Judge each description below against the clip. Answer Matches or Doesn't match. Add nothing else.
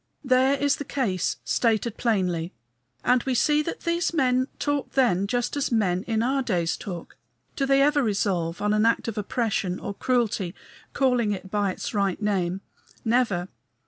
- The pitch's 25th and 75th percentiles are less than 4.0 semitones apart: Doesn't match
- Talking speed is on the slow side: Doesn't match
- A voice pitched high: Matches